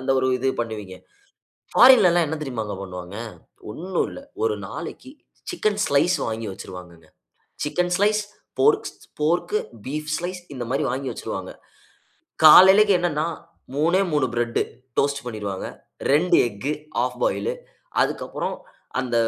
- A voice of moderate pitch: Yes, medium, 150 Hz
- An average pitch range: No, wide, 7.6 semitones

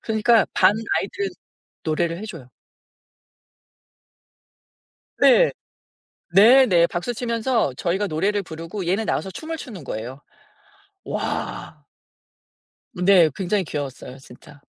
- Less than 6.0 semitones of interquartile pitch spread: Yes, wide, 5.5 semitones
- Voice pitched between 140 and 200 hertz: Yes, high, 190 Hz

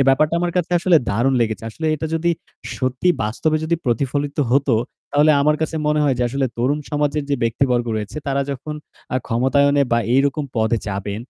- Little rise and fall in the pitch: No, average, 4.0 semitones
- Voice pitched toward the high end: No, medium, 140 Hz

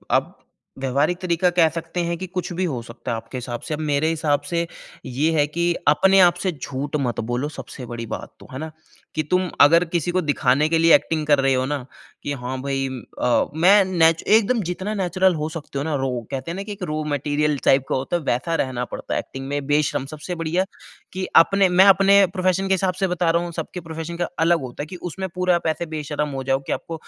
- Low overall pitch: No, medium, 160 Hz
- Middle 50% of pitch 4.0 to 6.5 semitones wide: Yes, average, 4.3 semitones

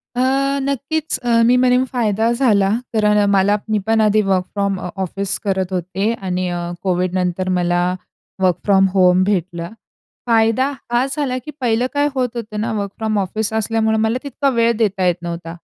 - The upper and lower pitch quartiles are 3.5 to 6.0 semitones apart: Yes, average, 3.9 semitones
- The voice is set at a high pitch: Yes, high, 210 Hz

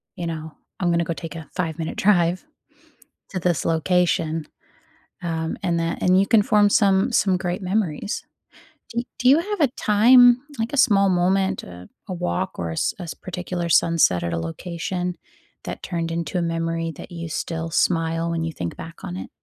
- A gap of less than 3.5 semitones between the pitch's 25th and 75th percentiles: Yes, average, 2.8 semitones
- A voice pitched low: No, medium, 175 Hz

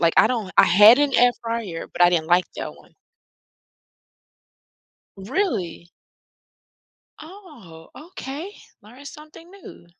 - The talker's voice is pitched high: Yes, high, 230 Hz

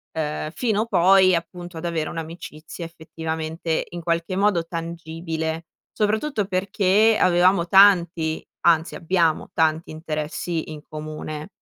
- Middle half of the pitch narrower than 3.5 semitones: Yes, narrow, 2.6 semitones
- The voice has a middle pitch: Yes, medium, 170 Hz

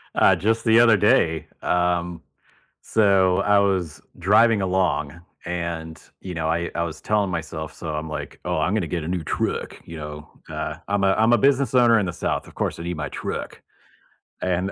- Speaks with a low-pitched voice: Yes, very low, 90 Hz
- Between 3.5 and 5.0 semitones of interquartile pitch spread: Yes, average, 3.8 semitones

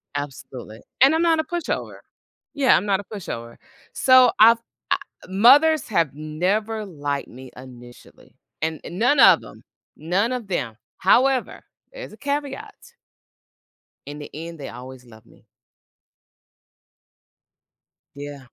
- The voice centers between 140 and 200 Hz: Yes, medium, 185 Hz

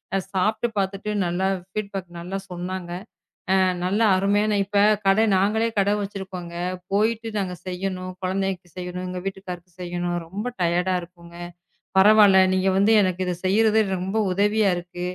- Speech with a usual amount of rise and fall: No, narrow, 2.1 semitones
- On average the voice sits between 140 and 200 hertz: Yes, high, 190 Hz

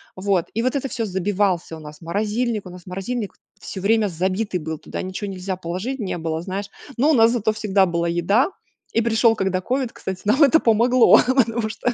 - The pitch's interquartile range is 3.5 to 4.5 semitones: Yes, average, 4.0 semitones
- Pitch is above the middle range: Yes, high, 205 Hz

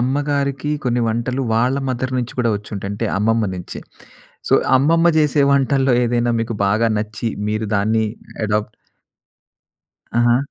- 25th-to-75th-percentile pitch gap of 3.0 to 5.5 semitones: Yes, average, 3.5 semitones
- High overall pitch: No, low, 120 Hz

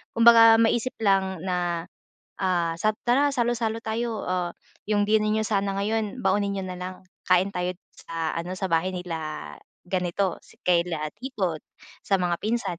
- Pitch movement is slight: No, average, 3.7 semitones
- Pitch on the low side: No, high, 190 Hz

